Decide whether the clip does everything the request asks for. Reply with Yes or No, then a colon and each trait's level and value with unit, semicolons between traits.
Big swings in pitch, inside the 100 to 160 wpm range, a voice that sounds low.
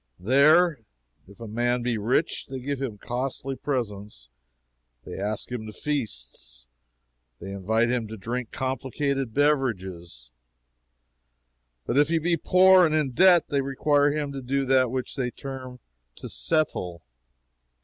No: average, 4.6 semitones; average, 140 wpm; low, 130 Hz